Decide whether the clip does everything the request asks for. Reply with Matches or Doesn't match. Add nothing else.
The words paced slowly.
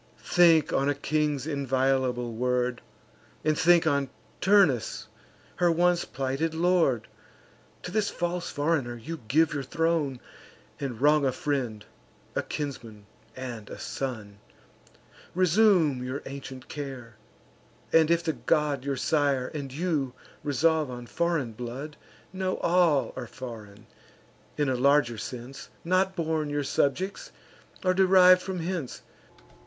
Matches